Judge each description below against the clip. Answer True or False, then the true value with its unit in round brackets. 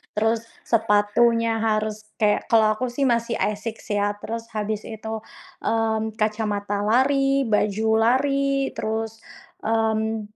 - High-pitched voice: True (220 Hz)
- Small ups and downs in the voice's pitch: True (1.3 semitones)